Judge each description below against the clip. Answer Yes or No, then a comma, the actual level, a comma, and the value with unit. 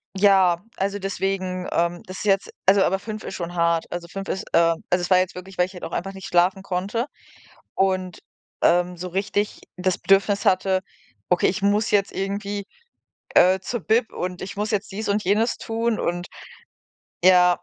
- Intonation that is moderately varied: No, narrow, 2.1 semitones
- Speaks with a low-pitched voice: No, high, 190 Hz